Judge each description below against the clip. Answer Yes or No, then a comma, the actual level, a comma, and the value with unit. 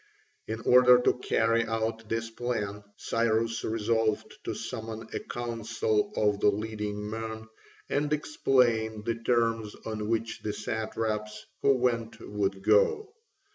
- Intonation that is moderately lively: No, narrow, 1.4 semitones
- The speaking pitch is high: No, low, 110 Hz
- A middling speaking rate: No, slow, 130 wpm